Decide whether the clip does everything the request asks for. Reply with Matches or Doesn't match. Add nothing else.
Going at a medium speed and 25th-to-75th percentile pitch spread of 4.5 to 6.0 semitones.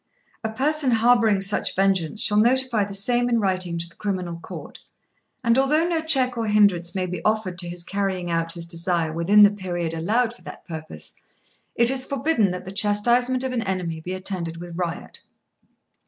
Matches